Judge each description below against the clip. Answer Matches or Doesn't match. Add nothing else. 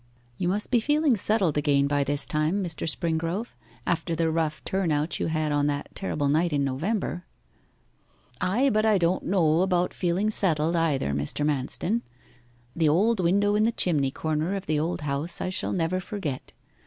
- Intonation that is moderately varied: Matches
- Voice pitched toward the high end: Doesn't match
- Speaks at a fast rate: Doesn't match